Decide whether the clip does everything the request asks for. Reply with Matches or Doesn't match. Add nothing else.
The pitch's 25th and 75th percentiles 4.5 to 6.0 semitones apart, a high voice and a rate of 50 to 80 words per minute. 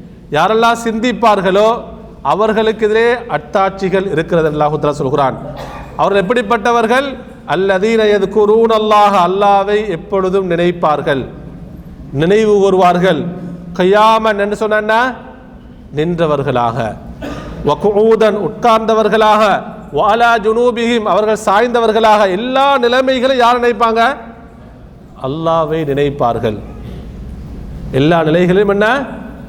Matches